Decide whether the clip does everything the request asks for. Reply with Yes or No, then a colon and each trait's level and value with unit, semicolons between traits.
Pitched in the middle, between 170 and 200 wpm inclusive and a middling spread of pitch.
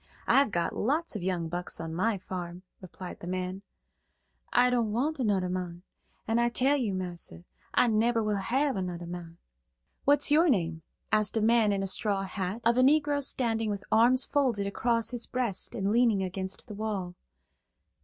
No: high, 210 Hz; average, 175 wpm; average, 4.7 semitones